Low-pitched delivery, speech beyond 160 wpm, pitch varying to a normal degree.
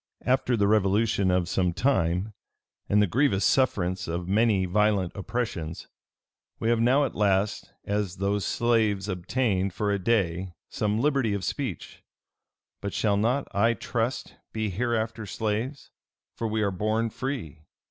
No: low, 105 Hz; average, 145 wpm; average, 3.4 semitones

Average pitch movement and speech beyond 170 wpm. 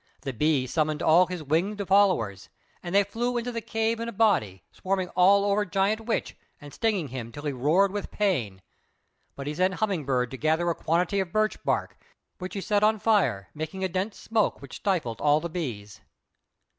No: wide, 5.8 semitones; average, 195 wpm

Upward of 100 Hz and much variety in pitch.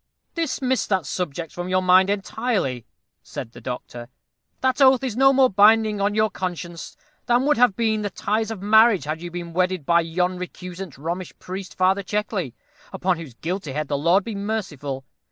No: medium, 185 Hz; average, 4.4 semitones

